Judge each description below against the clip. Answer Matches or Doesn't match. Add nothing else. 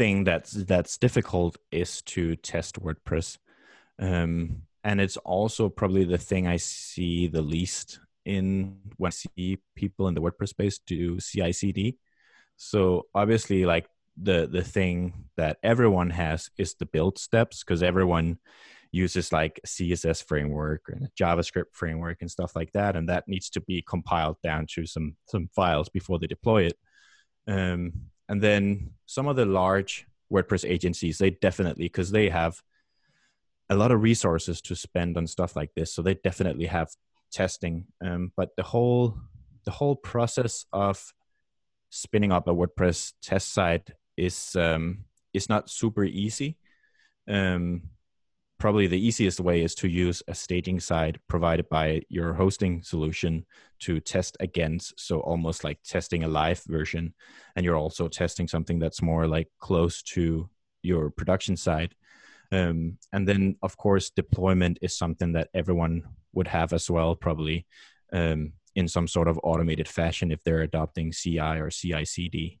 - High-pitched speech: Doesn't match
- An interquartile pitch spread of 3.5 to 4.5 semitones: Doesn't match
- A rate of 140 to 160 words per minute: Matches